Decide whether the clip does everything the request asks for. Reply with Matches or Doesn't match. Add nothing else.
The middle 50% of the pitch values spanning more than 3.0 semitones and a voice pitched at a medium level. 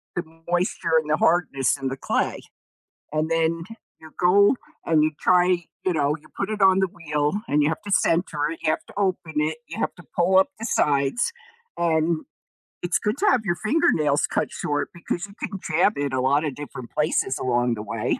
Matches